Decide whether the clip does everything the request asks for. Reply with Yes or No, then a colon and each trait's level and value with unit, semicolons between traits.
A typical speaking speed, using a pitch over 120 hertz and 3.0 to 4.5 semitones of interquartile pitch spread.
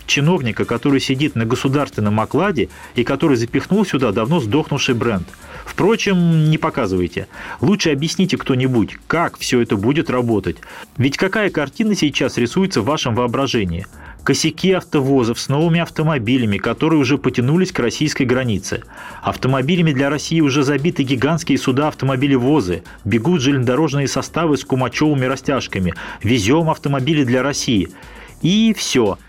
Yes: average, 130 wpm; medium, 140 Hz; average, 4.2 semitones